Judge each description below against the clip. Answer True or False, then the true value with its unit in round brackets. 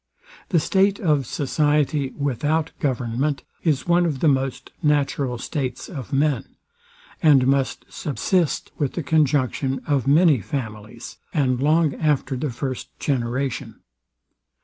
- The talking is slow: True (125 wpm)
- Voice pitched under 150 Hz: True (140 Hz)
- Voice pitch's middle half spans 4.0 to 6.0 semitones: False (2.7 semitones)